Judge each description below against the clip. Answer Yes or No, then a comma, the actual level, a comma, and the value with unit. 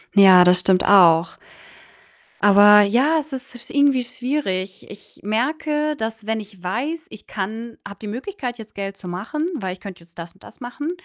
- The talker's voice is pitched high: Yes, high, 215 Hz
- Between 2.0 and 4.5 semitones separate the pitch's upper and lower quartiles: No, wide, 5.4 semitones